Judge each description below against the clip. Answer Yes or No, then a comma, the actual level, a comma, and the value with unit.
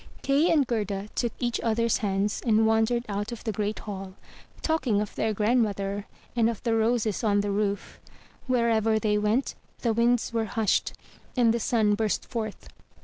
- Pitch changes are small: Yes, narrow, 2.1 semitones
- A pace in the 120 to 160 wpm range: No, average, 170 wpm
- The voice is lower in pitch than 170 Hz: No, high, 220 Hz